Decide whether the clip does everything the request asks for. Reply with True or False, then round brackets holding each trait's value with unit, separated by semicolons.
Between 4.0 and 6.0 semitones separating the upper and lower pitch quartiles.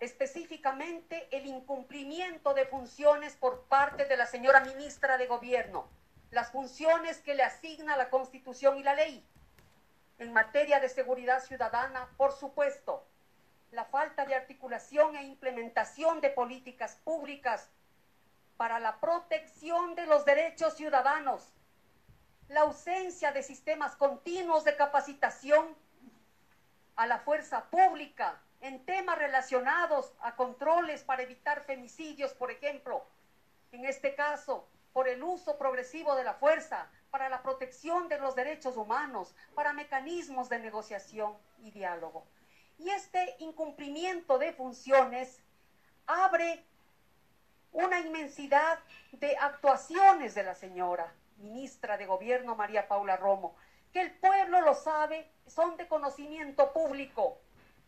False (3.4 semitones)